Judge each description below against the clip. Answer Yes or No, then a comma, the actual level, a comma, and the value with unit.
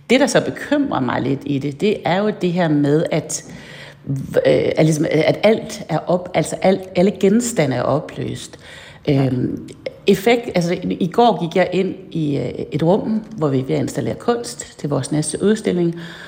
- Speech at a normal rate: Yes, average, 160 wpm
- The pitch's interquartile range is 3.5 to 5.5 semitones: Yes, average, 5.2 semitones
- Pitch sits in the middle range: Yes, medium, 175 Hz